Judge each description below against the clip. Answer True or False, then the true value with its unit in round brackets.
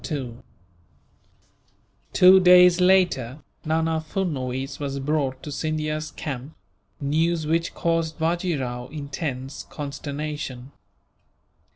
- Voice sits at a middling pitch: True (155 Hz)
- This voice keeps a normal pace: False (85 wpm)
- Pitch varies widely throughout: False (3.2 semitones)